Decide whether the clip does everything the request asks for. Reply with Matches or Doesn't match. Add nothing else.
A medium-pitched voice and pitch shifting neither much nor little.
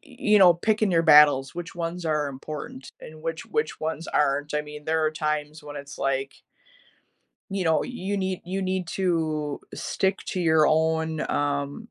Matches